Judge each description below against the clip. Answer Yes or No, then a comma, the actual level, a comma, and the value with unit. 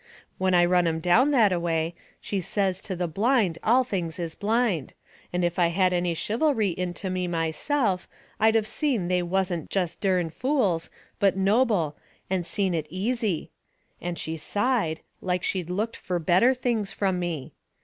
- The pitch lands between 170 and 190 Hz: Yes, medium, 185 Hz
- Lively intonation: No, average, 3.7 semitones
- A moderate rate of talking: Yes, average, 170 wpm